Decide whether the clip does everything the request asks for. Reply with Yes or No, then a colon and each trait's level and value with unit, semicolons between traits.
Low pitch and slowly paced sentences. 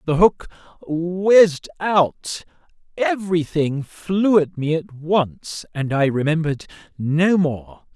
No: medium, 160 Hz; slow, 115 wpm